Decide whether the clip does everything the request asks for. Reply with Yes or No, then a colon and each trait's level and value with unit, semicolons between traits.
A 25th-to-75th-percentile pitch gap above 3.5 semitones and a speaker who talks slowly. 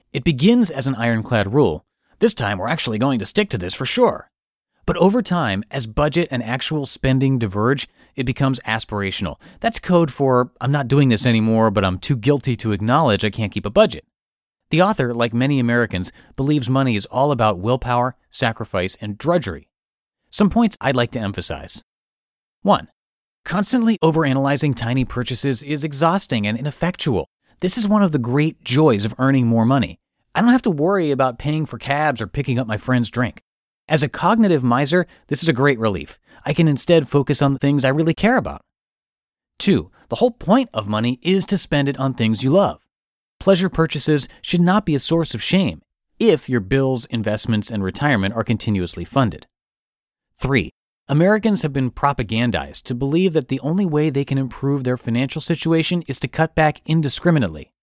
No: wide, 5.4 semitones; average, 185 wpm